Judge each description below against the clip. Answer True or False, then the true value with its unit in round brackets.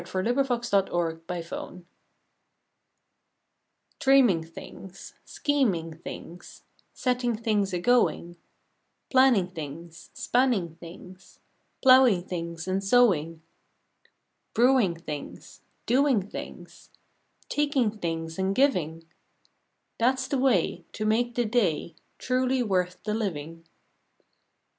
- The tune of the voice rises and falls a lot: True (6.6 semitones)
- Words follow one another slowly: True (95 wpm)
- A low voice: False (195 Hz)